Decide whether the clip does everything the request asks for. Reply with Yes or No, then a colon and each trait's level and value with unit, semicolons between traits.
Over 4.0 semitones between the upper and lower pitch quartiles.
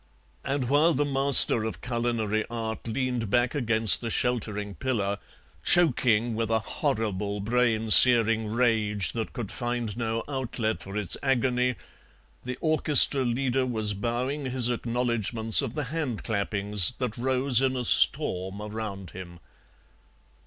No: average, 2.9 semitones